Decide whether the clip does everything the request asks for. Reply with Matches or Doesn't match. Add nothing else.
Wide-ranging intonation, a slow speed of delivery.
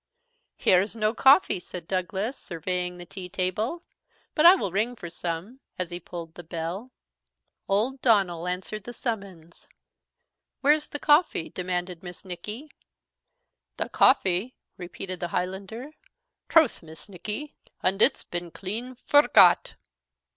Doesn't match